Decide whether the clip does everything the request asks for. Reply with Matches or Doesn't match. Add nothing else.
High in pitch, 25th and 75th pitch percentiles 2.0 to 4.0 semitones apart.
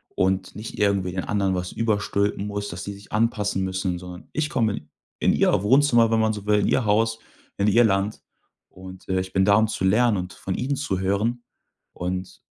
Doesn't match